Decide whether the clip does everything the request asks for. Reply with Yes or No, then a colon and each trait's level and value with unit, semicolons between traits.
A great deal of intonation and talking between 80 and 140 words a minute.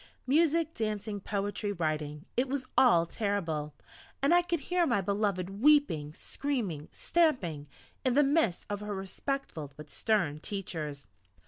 Yes: wide, 8.7 semitones; slow, 135 wpm